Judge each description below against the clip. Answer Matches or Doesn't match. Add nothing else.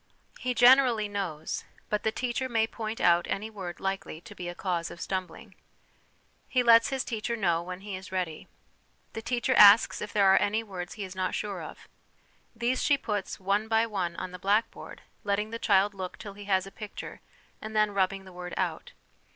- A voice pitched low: Doesn't match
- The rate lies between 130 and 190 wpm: Doesn't match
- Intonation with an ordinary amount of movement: Matches